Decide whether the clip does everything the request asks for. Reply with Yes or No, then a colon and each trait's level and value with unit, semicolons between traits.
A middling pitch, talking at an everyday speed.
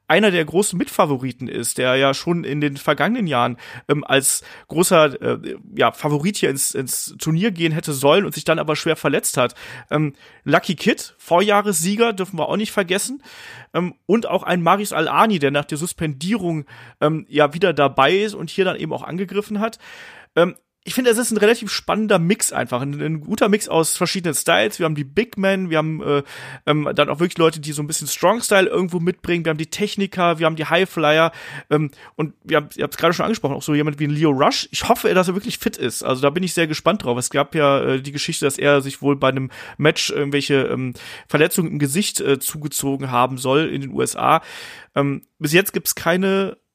No: medium, 160 Hz; fast, 215 wpm